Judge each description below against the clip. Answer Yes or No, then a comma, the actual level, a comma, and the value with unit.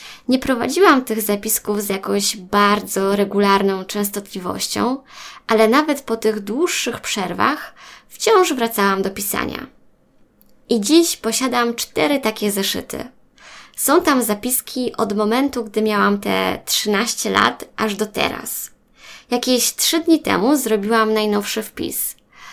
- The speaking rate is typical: Yes, average, 120 wpm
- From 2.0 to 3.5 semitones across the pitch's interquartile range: No, average, 4.2 semitones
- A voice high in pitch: Yes, high, 220 Hz